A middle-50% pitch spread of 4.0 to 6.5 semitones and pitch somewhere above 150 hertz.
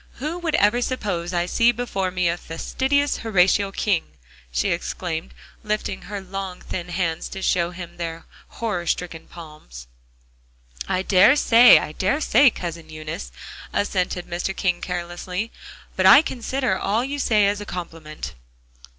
Yes: average, 4.4 semitones; medium, 185 Hz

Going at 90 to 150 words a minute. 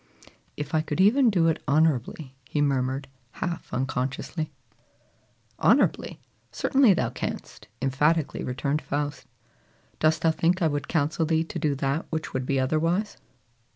Yes: average, 140 wpm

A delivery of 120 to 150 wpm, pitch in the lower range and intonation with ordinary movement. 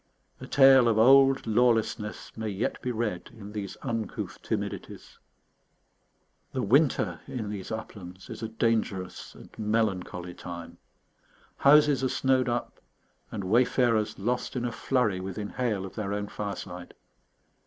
Yes: slow, 135 wpm; low, 110 Hz; average, 4.0 semitones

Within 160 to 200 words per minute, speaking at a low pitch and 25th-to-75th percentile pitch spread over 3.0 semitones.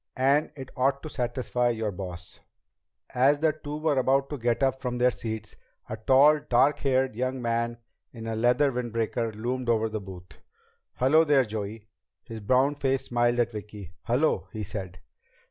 Yes: average, 170 wpm; low, 120 Hz; average, 3.4 semitones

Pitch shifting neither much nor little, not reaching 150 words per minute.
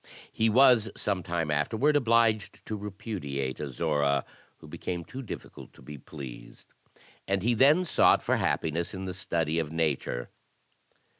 No: wide, 6.9 semitones; average, 140 wpm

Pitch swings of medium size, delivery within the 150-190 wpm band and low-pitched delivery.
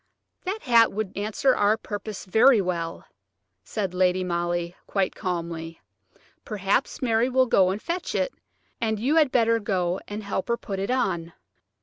No: average, 4.4 semitones; average, 155 wpm; high, 205 Hz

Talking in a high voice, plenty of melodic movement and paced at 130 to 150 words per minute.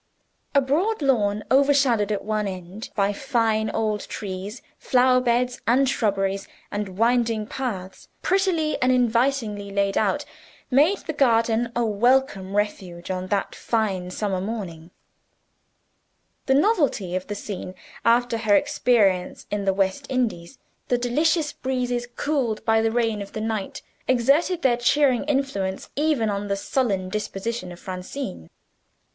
No: high, 225 Hz; average, 4.5 semitones; average, 140 wpm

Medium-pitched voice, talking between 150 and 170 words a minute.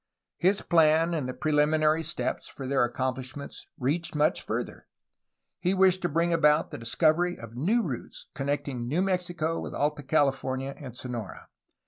Yes: medium, 150 Hz; average, 155 wpm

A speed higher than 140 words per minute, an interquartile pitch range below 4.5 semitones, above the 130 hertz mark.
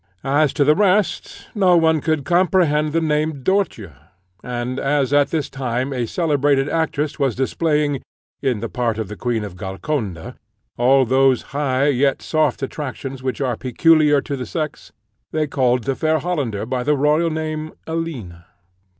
Yes: average, 160 wpm; average, 3.7 semitones; medium, 140 Hz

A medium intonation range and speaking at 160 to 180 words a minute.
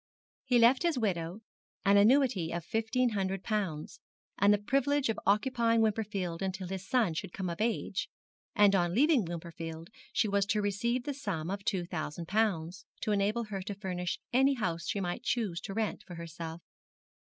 Yes: average, 4.5 semitones; average, 175 wpm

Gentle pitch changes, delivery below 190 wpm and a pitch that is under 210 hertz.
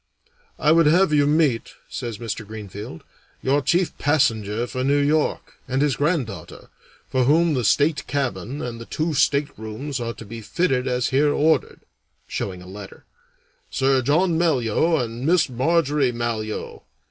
No: average, 4.5 semitones; average, 150 wpm; low, 135 Hz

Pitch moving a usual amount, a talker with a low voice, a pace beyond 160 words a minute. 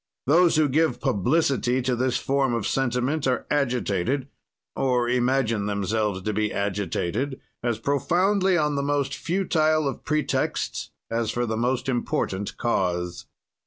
No: average, 4.6 semitones; low, 125 Hz; slow, 135 wpm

